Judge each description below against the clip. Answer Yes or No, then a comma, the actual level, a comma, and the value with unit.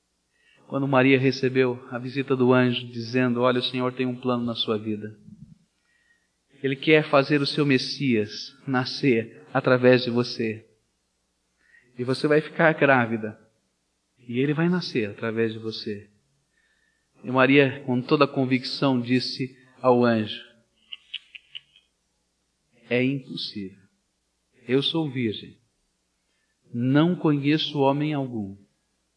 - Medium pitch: No, low, 125 Hz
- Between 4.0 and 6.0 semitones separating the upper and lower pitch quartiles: No, average, 3.6 semitones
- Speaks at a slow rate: Yes, slow, 115 wpm